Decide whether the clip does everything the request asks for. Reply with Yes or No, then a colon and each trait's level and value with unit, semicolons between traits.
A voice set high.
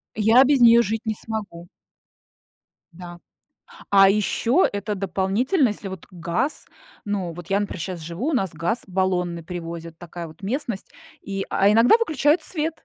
Yes: high, 195 Hz